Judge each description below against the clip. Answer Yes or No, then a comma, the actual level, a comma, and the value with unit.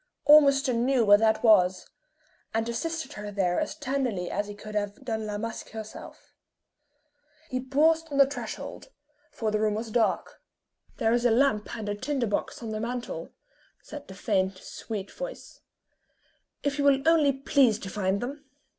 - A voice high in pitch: Yes, high, 230 Hz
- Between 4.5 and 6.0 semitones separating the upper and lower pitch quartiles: Yes, average, 4.9 semitones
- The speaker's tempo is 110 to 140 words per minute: No, average, 170 wpm